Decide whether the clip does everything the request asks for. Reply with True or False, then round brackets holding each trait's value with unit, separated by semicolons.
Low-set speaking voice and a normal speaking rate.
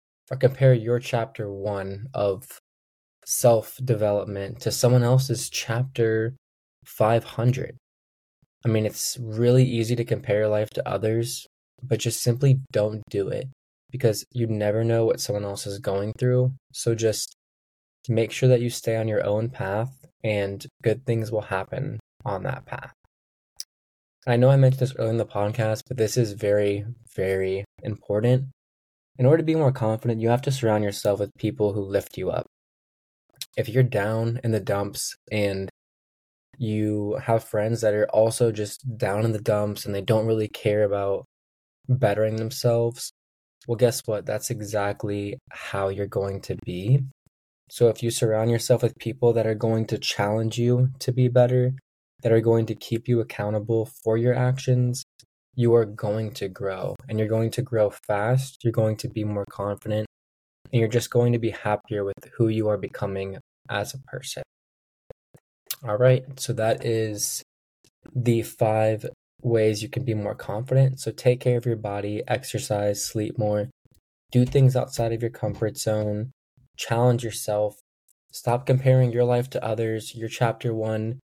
True (110 Hz; 165 wpm)